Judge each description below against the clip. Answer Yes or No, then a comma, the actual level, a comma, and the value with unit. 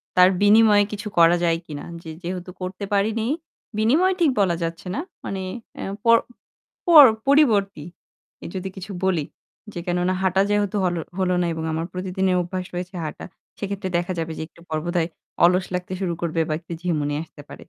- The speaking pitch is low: No, medium, 185 Hz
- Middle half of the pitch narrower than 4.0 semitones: Yes, average, 2.8 semitones